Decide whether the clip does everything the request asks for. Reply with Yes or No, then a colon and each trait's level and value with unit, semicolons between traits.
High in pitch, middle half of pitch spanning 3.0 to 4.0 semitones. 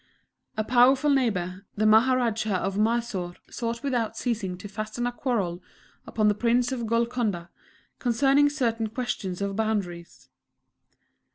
Yes: high, 225 Hz; average, 3.5 semitones